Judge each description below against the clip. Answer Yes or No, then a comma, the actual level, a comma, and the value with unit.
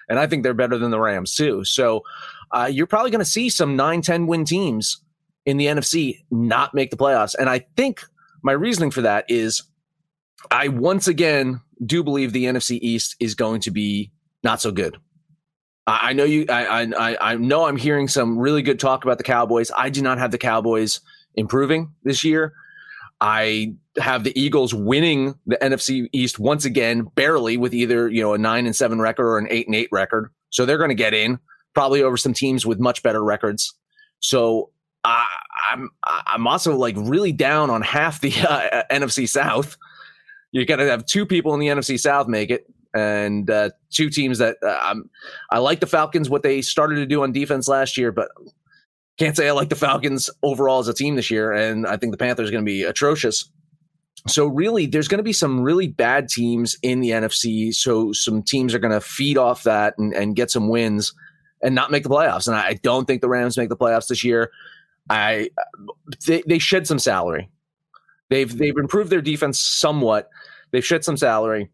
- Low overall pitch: Yes, low, 130 Hz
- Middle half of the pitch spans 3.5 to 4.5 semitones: No, average, 4.9 semitones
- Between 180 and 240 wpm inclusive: Yes, fast, 205 wpm